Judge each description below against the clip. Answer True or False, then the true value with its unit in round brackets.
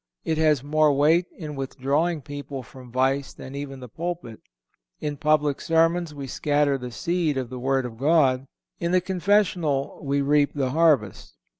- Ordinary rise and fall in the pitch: True (3.3 semitones)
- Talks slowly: False (165 wpm)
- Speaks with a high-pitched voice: False (145 Hz)